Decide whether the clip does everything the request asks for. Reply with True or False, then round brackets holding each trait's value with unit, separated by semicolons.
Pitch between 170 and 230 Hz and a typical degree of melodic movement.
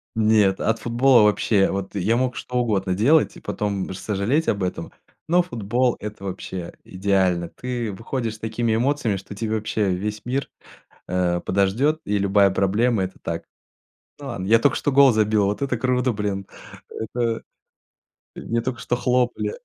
False (110 Hz; 4.0 semitones)